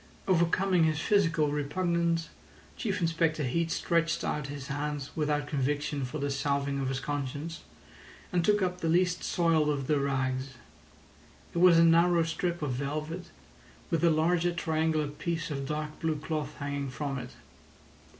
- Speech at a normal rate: Yes, average, 155 wpm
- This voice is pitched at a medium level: Yes, medium, 155 Hz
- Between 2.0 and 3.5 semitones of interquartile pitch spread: Yes, average, 2.9 semitones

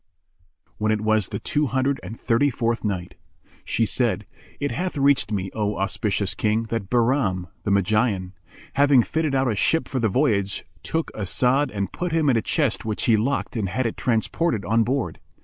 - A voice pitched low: Yes, low, 115 Hz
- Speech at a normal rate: Yes, average, 185 wpm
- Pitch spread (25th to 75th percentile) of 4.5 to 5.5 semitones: Yes, average, 4.9 semitones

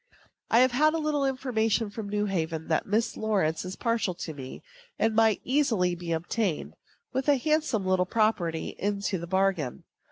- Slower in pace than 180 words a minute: Yes, average, 165 wpm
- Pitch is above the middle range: Yes, high, 210 Hz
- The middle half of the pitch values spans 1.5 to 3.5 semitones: No, wide, 5.4 semitones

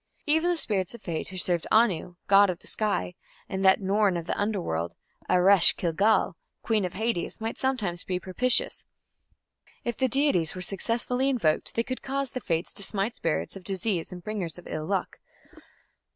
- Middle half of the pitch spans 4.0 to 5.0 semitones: Yes, average, 4.7 semitones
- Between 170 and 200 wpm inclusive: Yes, average, 180 wpm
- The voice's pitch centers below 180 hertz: No, high, 195 Hz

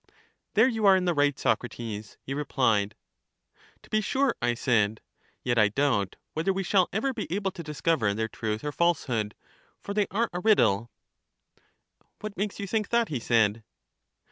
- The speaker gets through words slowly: No, average, 170 wpm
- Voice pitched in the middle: Yes, medium, 145 Hz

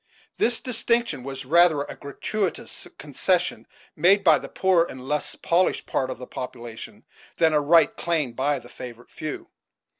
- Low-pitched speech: No, medium, 150 Hz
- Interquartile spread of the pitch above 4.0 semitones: Yes, average, 5.2 semitones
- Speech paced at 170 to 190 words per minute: No, average, 155 wpm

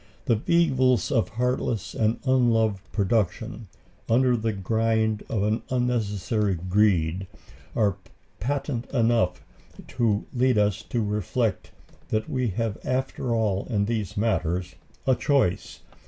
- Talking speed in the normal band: No, slow, 120 wpm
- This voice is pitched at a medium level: No, low, 110 Hz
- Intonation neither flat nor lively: Yes, average, 3.2 semitones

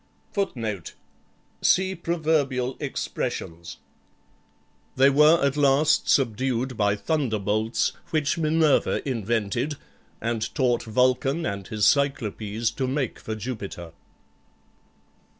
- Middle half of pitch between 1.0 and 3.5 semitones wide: No, average, 5.1 semitones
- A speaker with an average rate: No, slow, 95 wpm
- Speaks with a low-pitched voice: Yes, low, 130 Hz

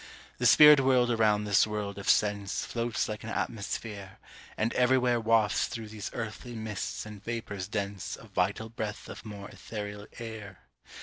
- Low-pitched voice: Yes, low, 110 Hz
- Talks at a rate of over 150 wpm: Yes, average, 160 wpm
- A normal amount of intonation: No, narrow, 2.1 semitones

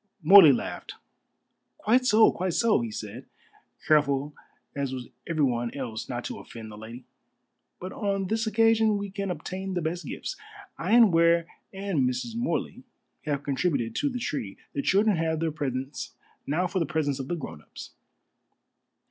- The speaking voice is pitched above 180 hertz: No, medium, 165 Hz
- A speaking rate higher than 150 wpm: Yes, average, 165 wpm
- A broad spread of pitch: Yes, wide, 6.9 semitones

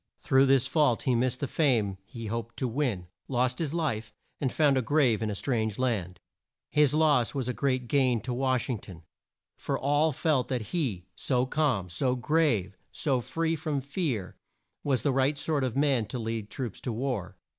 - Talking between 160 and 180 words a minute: No, average, 190 wpm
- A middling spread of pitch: Yes, average, 3.9 semitones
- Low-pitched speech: Yes, low, 130 Hz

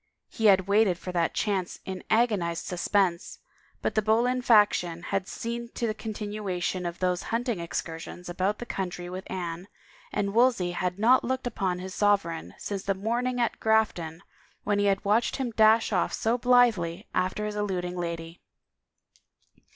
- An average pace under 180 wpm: Yes, average, 160 wpm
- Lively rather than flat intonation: No, average, 3.7 semitones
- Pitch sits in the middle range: No, high, 200 Hz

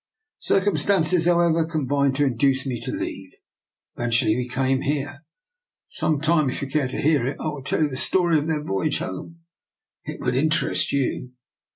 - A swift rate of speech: No, average, 185 wpm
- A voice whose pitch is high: No, medium, 145 Hz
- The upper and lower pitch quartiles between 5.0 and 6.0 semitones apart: No, average, 3.5 semitones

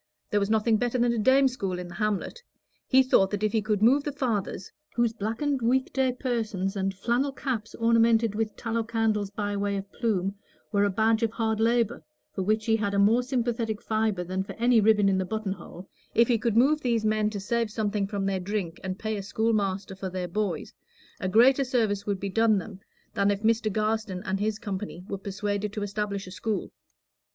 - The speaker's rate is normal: No, fast, 215 wpm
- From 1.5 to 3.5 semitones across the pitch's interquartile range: Yes, narrow, 2.6 semitones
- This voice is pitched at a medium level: No, high, 215 Hz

